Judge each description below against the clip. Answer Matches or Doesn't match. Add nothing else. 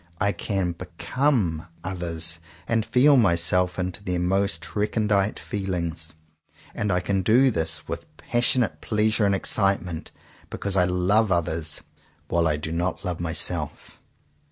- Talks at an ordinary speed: Doesn't match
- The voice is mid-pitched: Doesn't match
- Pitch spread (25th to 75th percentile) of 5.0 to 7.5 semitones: Doesn't match